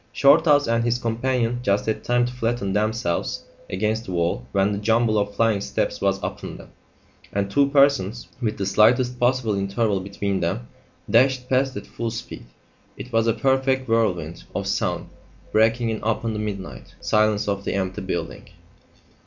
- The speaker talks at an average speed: Yes, average, 170 wpm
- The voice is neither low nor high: No, low, 110 Hz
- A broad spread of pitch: No, average, 3.6 semitones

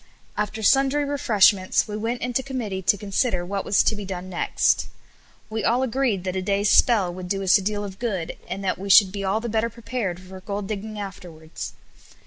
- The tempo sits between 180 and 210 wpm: Yes, fast, 205 wpm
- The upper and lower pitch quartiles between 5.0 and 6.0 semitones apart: No, average, 3.2 semitones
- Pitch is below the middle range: No, high, 205 Hz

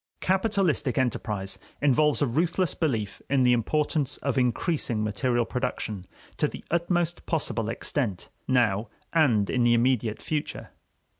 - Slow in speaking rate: Yes, slow, 130 wpm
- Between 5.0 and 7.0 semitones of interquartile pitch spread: Yes, average, 5.3 semitones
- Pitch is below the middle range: Yes, low, 130 Hz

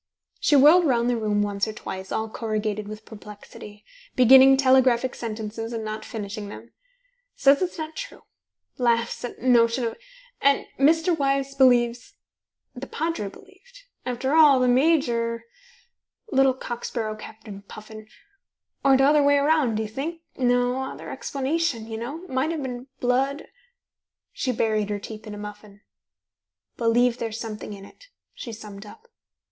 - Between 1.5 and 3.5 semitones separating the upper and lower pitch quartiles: No, average, 4.1 semitones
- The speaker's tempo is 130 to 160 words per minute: Yes, average, 150 wpm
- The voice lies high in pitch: Yes, high, 245 Hz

